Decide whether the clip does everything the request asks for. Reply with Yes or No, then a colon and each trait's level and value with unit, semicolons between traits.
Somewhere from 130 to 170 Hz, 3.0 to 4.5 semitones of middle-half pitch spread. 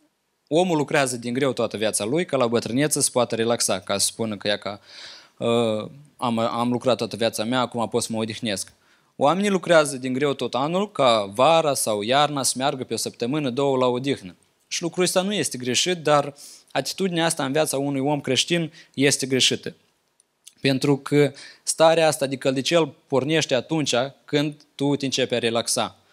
Yes: low, 135 Hz; average, 3.9 semitones